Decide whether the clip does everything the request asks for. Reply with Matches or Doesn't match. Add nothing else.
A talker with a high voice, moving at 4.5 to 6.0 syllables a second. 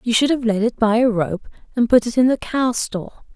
Matches